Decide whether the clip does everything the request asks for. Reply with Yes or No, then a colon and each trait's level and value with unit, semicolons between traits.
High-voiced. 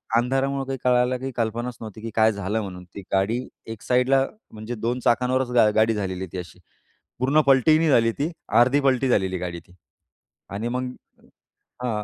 No: low, 120 Hz